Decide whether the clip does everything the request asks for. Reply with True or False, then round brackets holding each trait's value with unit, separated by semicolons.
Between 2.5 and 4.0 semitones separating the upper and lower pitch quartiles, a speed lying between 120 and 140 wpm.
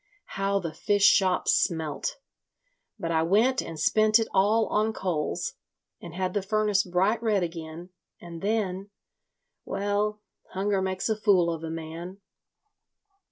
True (3.7 semitones; 135 wpm)